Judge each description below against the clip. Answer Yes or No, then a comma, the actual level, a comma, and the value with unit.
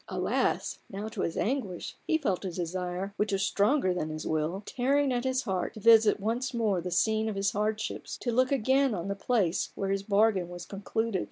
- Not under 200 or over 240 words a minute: Yes, fast, 205 wpm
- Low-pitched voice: No, high, 205 Hz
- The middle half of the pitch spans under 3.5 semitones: No, average, 4.0 semitones